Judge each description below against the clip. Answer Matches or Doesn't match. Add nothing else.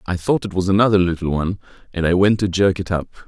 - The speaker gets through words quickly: Matches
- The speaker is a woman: Doesn't match